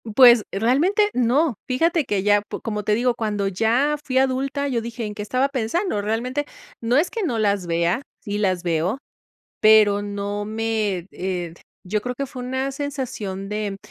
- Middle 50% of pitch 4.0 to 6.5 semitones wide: Yes, average, 4.3 semitones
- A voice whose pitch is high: Yes, high, 225 Hz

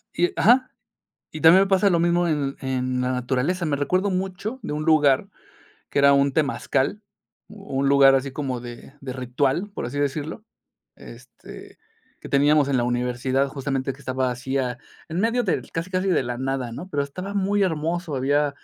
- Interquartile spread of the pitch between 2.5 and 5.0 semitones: No, wide, 5.4 semitones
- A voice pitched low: No, medium, 145 Hz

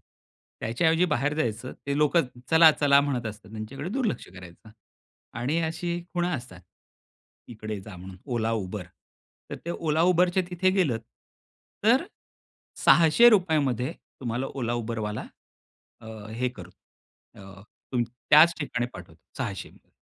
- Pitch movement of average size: No, wide, 6.9 semitones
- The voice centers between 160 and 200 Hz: No, low, 130 Hz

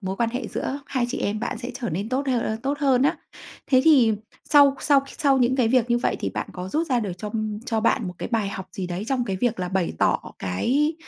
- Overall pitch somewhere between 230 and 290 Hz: Yes, high, 240 Hz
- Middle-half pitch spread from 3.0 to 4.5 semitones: No, average, 4.9 semitones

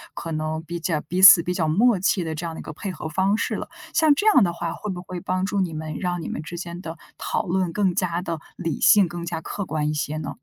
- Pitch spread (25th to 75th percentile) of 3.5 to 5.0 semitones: No, average, 2.7 semitones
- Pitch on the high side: No, medium, 175 Hz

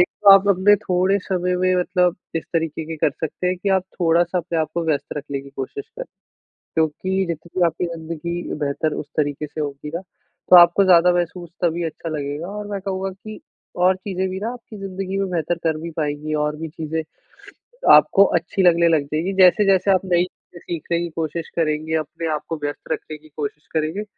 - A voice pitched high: No, medium, 170 Hz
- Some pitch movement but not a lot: Yes, average, 3.0 semitones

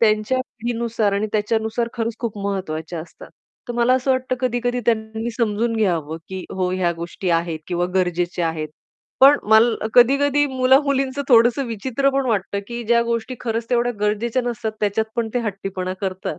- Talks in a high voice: Yes, high, 225 Hz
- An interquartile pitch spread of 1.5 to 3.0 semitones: No, average, 4.0 semitones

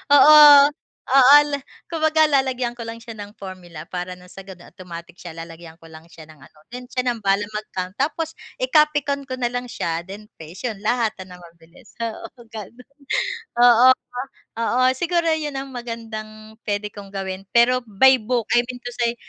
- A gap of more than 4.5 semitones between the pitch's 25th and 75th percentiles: Yes, average, 5.2 semitones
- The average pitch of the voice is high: Yes, high, 230 Hz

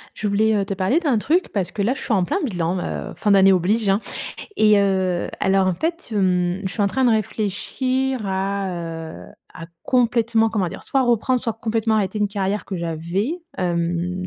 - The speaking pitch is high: Yes, high, 200 Hz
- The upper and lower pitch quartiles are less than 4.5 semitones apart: Yes, average, 3.6 semitones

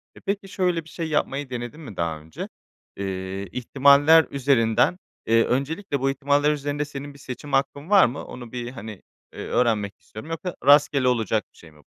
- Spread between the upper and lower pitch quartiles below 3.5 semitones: No, average, 4.4 semitones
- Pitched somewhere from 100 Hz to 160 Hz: Yes, low, 135 Hz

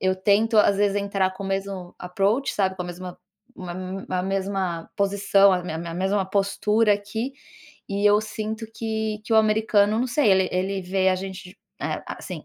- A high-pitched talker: Yes, high, 195 Hz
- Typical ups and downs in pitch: No, narrow, 2.1 semitones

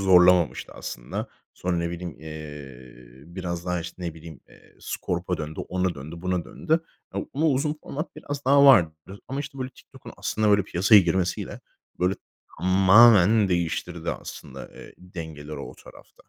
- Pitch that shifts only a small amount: No, average, 4.2 semitones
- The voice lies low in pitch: Yes, very low, 90 Hz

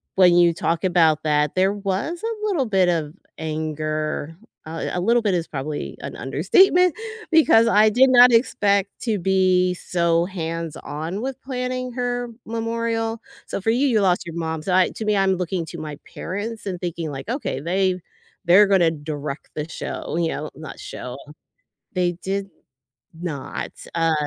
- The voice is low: No, medium, 185 Hz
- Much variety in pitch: Yes, wide, 5.8 semitones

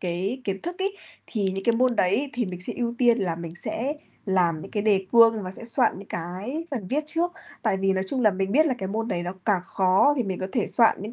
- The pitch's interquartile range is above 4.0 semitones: Yes, average, 4.7 semitones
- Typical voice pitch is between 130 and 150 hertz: No, high, 205 Hz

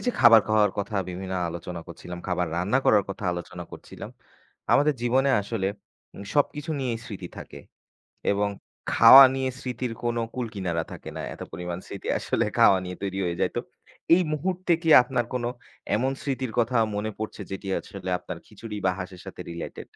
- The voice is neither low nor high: No, low, 110 Hz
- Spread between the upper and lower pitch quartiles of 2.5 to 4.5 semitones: No, wide, 5.6 semitones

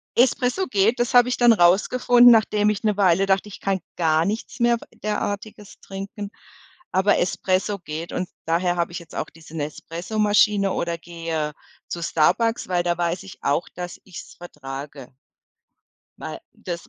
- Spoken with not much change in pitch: No, average, 3.8 semitones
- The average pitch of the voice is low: No, high, 190 Hz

